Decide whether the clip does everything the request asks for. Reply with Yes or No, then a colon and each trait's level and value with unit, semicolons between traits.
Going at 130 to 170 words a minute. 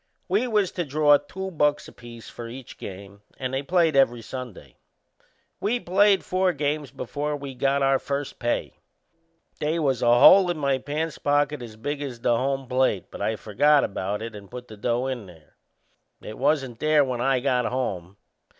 No: average, 185 wpm